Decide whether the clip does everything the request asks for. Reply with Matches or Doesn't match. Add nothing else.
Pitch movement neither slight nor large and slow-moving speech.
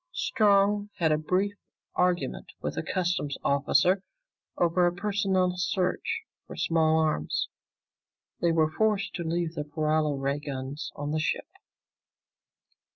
Matches